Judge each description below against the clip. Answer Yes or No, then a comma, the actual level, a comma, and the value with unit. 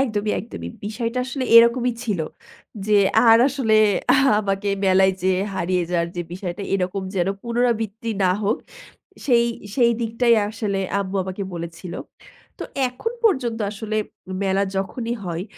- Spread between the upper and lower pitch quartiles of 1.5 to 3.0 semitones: No, average, 3.8 semitones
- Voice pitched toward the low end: No, high, 210 Hz